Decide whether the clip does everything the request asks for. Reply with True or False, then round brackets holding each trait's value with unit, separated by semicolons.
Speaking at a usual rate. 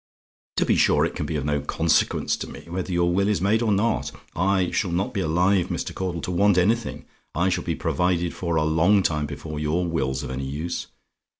False (220 wpm)